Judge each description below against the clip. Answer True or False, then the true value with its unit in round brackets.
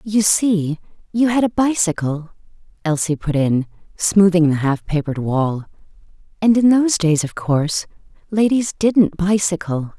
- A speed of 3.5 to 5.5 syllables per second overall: True (4.5 syllables/s)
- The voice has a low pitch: False (180 Hz)